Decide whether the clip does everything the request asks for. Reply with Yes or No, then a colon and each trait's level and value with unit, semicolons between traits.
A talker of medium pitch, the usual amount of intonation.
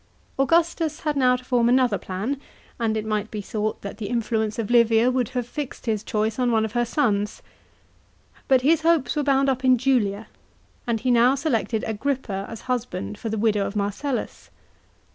No: high, 235 Hz; average, 3.4 semitones